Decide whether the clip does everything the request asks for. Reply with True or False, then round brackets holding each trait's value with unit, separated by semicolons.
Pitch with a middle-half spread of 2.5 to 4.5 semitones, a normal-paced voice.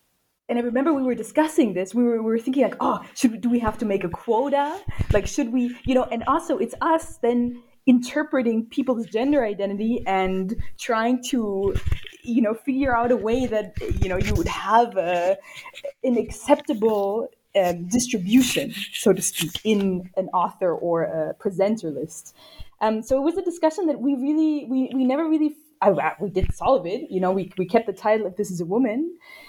False (5.2 semitones; 195 wpm)